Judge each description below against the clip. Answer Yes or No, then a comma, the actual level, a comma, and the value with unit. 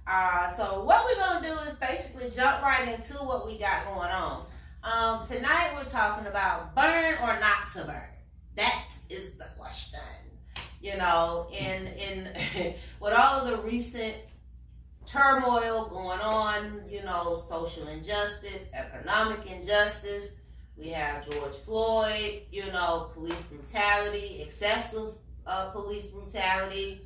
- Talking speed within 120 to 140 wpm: Yes, slow, 135 wpm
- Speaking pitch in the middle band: No, high, 205 Hz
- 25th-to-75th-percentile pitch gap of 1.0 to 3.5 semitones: No, average, 4.3 semitones